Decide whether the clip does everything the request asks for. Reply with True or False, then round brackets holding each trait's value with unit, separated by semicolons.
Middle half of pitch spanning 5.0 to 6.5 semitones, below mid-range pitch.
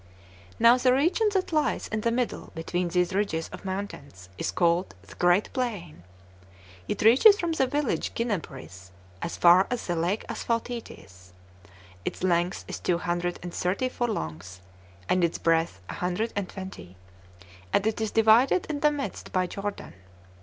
False (5.6 semitones; 190 Hz)